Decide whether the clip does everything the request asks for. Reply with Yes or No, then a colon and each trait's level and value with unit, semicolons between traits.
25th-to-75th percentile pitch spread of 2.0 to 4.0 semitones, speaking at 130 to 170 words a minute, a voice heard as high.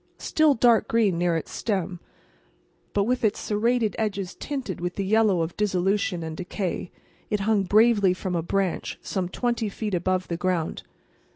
Yes: average, 3.5 semitones; average, 165 wpm; high, 195 Hz